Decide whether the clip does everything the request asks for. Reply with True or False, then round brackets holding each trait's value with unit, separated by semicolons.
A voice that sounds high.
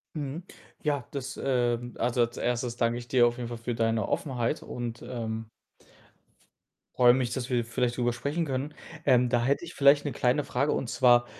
False (125 Hz)